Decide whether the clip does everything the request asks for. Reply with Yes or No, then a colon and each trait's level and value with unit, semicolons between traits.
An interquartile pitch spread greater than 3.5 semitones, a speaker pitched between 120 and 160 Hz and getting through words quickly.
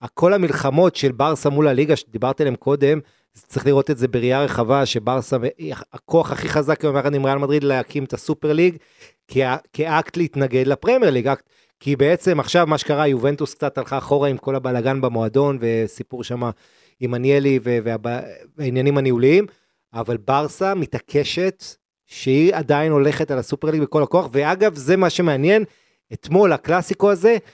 No: average, 3.0 semitones; medium, 140 Hz; fast, 155 wpm